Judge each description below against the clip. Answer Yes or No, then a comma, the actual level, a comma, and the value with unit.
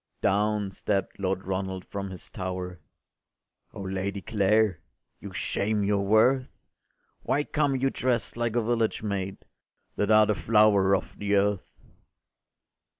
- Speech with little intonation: Yes, narrow, 2.3 semitones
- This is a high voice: No, low, 100 Hz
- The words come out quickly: No, slow, 135 wpm